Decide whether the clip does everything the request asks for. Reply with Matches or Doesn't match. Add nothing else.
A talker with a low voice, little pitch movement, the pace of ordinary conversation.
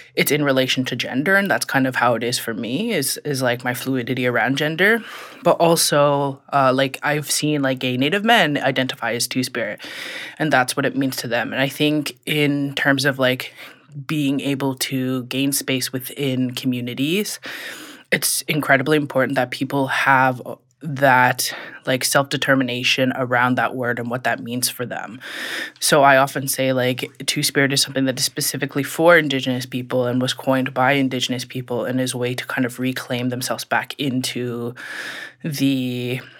Matches